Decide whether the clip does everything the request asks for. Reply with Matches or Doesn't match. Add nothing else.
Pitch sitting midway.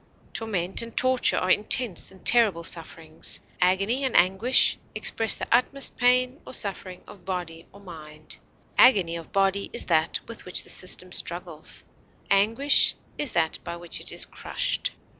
Doesn't match